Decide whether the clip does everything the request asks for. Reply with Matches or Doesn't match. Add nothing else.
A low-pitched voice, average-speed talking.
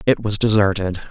Matches